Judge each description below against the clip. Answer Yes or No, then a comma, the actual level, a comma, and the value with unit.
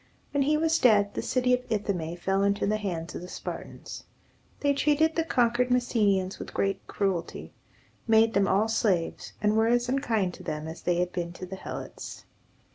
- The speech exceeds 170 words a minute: Yes, average, 190 wpm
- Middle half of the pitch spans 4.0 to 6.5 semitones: Yes, average, 5.2 semitones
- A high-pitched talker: Yes, high, 210 Hz